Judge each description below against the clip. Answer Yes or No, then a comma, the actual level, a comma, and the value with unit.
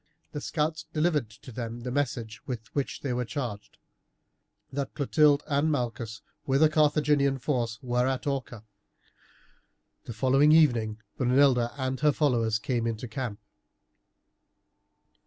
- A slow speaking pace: Yes, slow, 130 wpm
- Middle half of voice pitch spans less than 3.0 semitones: No, average, 3.6 semitones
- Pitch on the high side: No, low, 130 Hz